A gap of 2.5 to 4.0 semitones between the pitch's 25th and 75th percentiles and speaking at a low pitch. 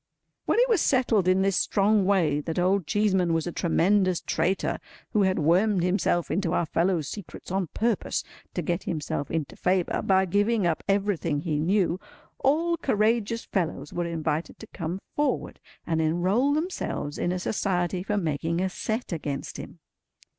No: average, 3.7 semitones; medium, 185 Hz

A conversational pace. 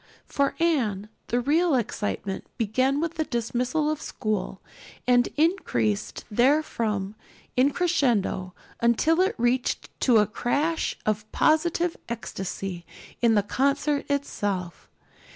No: slow, 115 wpm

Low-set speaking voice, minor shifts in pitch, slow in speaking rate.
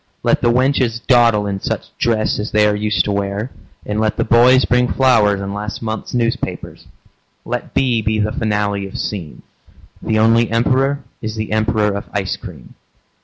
No: low, 110 Hz; narrow, 2.3 semitones; average, 175 wpm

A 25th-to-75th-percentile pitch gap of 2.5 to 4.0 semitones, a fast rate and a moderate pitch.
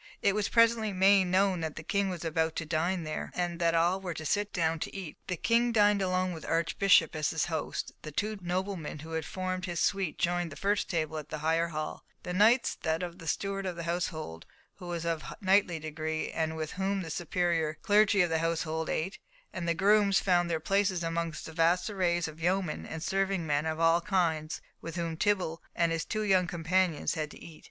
Yes: average, 3.0 semitones; fast, 220 wpm; medium, 170 Hz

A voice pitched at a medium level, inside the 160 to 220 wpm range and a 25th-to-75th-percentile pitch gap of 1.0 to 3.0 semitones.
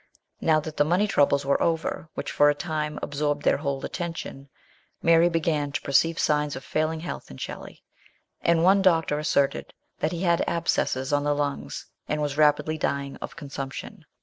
Yes: medium, 150 Hz; average, 175 wpm; narrow, 2.4 semitones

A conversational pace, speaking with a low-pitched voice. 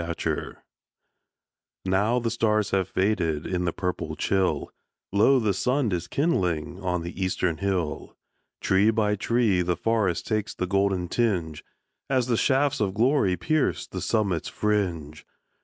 Yes: average, 145 wpm; low, 100 Hz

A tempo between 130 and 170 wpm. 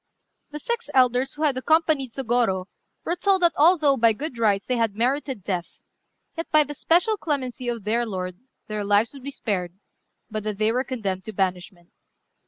No: average, 185 wpm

